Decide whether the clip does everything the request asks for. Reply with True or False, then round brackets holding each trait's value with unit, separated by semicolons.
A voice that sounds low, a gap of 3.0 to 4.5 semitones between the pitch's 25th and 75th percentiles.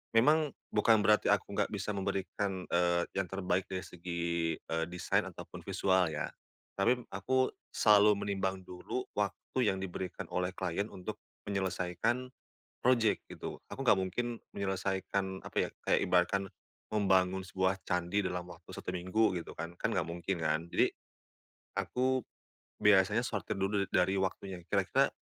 False (95 Hz; 2.4 semitones)